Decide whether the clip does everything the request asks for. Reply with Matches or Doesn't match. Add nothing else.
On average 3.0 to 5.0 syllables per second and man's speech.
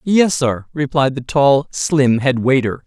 Matches